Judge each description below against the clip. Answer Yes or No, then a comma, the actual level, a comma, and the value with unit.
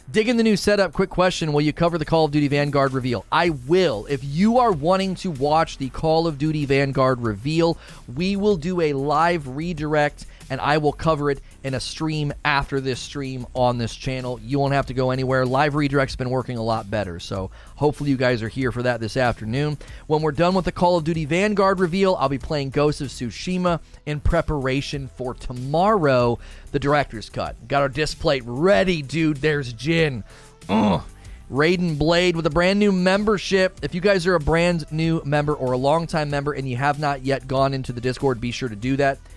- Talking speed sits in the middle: No, fast, 210 wpm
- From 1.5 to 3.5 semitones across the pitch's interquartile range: No, average, 4.2 semitones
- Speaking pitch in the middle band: Yes, medium, 145 Hz